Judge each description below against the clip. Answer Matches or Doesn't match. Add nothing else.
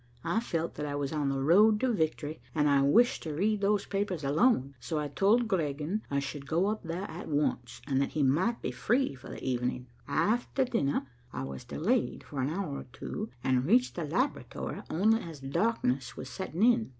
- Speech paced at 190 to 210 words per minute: Matches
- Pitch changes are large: Matches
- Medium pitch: Matches